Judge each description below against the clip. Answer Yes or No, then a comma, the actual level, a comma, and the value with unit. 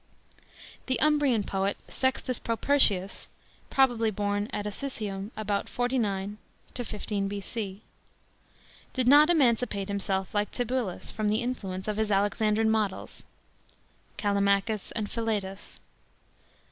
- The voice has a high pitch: Yes, high, 210 Hz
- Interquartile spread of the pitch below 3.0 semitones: No, average, 3.4 semitones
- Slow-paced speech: Yes, slow, 105 wpm